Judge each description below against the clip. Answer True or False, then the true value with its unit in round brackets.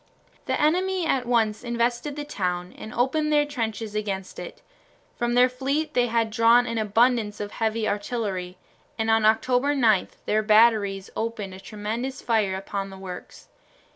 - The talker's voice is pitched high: True (225 Hz)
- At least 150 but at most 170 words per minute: True (160 wpm)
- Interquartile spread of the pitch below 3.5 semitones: True (3.0 semitones)